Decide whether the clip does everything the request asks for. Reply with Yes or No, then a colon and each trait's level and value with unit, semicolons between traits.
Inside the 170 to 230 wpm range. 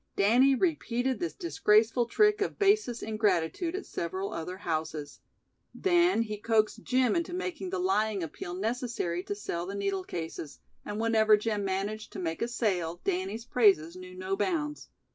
No: average, 160 wpm